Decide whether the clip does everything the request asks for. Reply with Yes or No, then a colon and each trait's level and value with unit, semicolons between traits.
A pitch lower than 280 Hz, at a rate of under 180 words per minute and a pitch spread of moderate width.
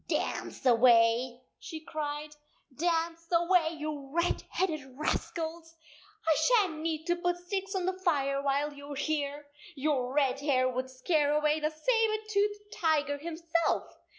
No: very high, 310 Hz; average, 155 wpm; average, 3.3 semitones